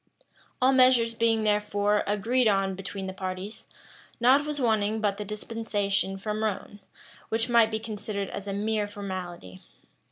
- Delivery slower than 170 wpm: Yes, average, 150 wpm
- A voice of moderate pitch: No, high, 210 Hz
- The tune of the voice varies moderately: No, narrow, 2.3 semitones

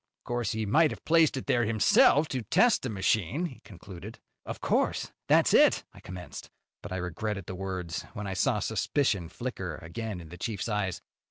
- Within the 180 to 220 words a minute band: Yes, average, 190 wpm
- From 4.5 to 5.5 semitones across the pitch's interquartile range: Yes, average, 5.1 semitones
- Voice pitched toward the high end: No, low, 105 Hz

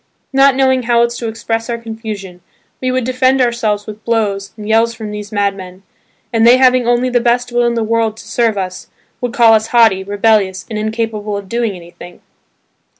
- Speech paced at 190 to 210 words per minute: Yes, average, 195 wpm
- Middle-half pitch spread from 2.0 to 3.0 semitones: Yes, narrow, 2.6 semitones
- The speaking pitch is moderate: No, high, 225 Hz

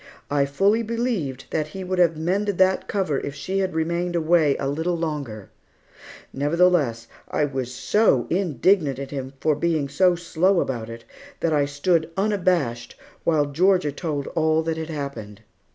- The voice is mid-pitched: Yes, medium, 160 Hz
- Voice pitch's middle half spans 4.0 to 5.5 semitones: Yes, average, 4.4 semitones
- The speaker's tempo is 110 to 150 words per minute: No, average, 160 wpm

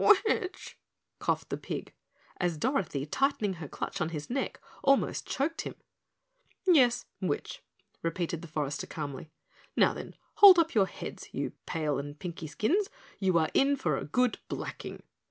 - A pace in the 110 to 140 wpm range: No, average, 155 wpm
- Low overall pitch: No, medium, 185 Hz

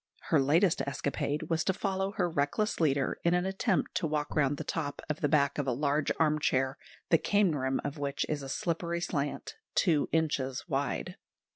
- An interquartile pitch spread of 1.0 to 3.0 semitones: No, average, 3.5 semitones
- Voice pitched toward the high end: No, medium, 150 Hz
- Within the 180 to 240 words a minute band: Yes, average, 185 wpm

